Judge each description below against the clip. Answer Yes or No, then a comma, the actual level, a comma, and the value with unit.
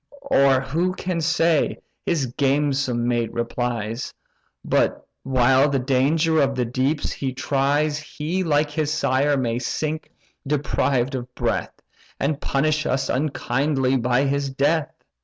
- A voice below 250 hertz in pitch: Yes, medium, 140 Hz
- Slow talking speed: Yes, slow, 130 wpm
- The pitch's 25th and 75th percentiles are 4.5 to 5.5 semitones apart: No, average, 2.9 semitones